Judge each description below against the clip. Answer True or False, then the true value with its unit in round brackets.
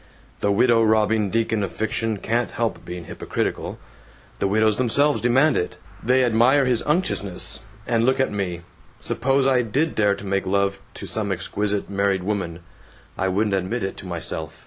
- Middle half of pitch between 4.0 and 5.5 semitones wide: False (3.6 semitones)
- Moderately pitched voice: False (110 Hz)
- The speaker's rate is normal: True (170 wpm)